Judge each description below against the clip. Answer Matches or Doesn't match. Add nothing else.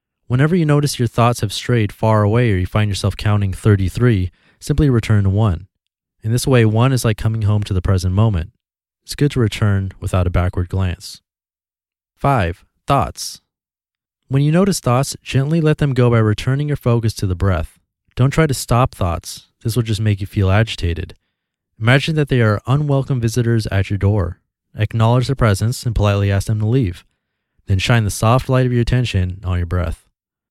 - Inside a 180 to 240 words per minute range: Matches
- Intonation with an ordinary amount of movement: Matches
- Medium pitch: Doesn't match